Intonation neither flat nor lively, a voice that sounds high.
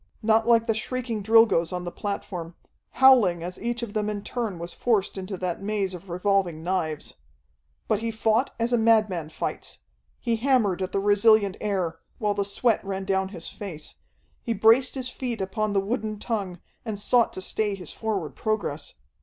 Yes: average, 3.3 semitones; high, 205 Hz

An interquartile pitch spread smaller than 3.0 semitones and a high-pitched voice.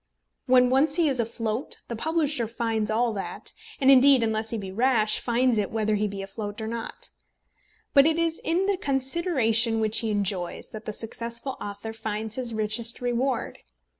No: average, 3.4 semitones; high, 230 Hz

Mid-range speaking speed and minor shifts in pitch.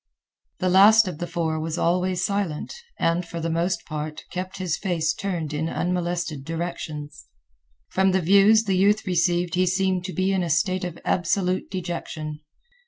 Yes: average, 170 wpm; narrow, 2.3 semitones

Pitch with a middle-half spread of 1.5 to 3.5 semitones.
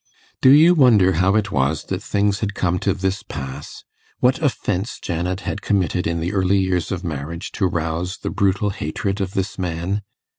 Yes: average, 3.2 semitones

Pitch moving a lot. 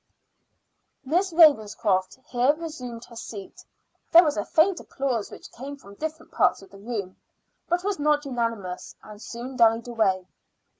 Yes: wide, 6.2 semitones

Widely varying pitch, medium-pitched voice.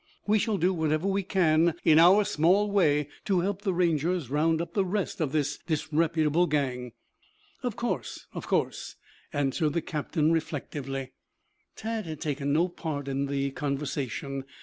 No: average, 3.9 semitones; medium, 155 Hz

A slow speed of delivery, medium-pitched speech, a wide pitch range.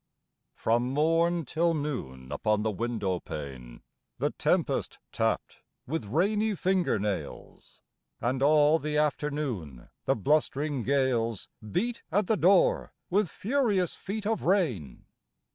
Yes: slow, 120 wpm; medium, 145 Hz; wide, 8.0 semitones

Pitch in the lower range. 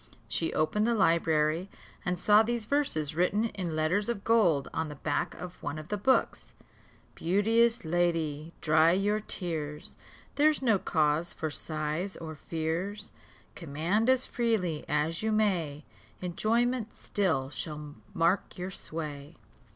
No: medium, 175 Hz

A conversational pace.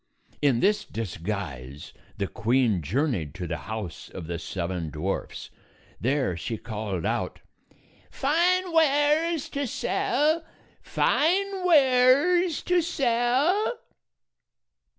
No: slow, 100 wpm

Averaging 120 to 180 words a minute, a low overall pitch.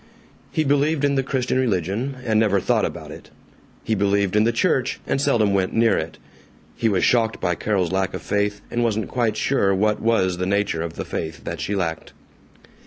No: average, 200 wpm; low, 105 Hz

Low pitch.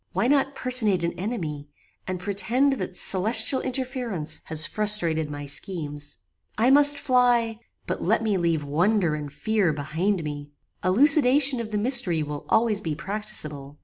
No: high, 200 Hz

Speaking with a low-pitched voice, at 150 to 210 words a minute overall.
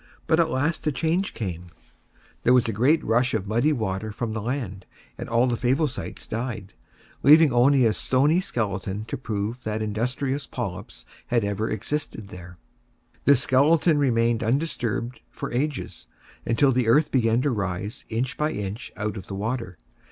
Yes: low, 120 Hz; average, 165 wpm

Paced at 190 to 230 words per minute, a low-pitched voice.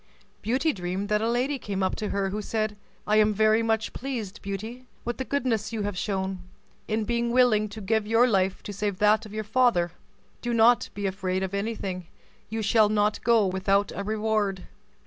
No: average, 195 wpm; high, 215 Hz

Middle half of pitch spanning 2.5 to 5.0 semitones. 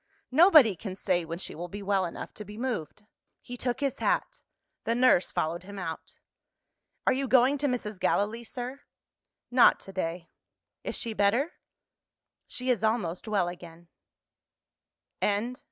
No: wide, 5.4 semitones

